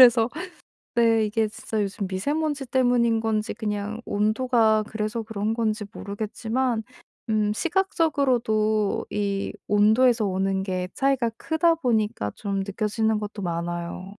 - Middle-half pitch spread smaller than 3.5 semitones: Yes, narrow, 2.6 semitones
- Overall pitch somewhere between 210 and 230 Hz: Yes, high, 220 Hz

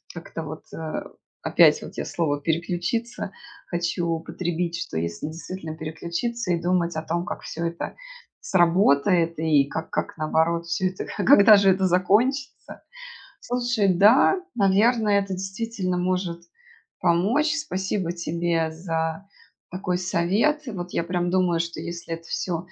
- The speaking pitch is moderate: Yes, medium, 175 Hz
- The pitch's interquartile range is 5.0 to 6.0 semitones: No, average, 2.9 semitones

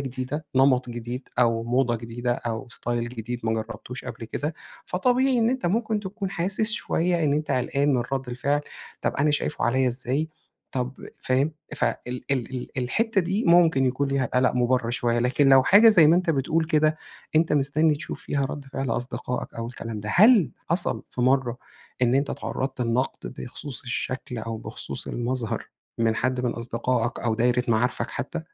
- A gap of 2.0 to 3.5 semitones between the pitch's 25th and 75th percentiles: No, average, 4.2 semitones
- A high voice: No, low, 130 Hz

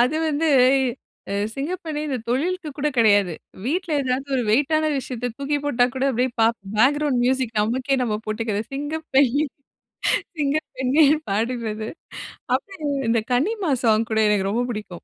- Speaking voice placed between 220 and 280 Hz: Yes, very high, 260 Hz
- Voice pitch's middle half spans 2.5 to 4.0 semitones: No, average, 4.5 semitones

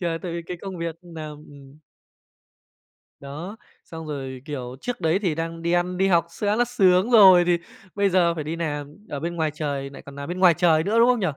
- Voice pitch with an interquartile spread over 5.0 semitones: No, average, 3.5 semitones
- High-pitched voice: No, medium, 170 Hz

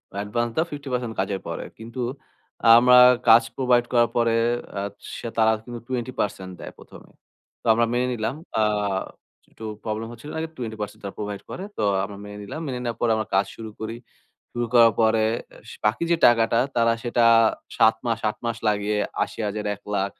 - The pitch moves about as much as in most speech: No, narrow, 2.2 semitones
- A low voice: Yes, low, 115 Hz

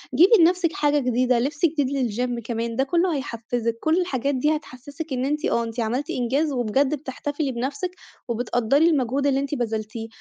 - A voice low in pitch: No, very high, 265 Hz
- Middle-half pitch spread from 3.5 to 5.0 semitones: Yes, average, 3.8 semitones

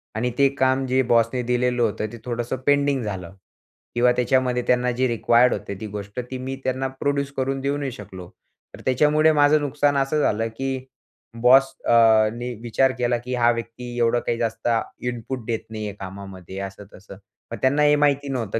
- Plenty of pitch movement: No, average, 2.8 semitones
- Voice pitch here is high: No, low, 125 Hz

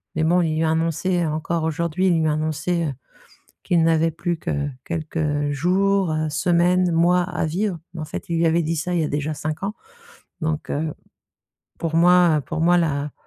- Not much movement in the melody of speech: Yes, narrow, 2.0 semitones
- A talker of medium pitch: Yes, medium, 165 Hz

